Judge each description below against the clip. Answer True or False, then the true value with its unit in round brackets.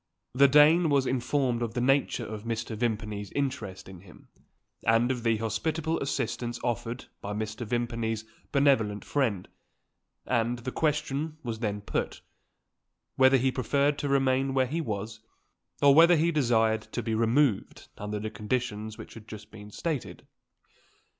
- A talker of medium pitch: False (120 Hz)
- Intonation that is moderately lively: True (4.0 semitones)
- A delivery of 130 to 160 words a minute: True (150 wpm)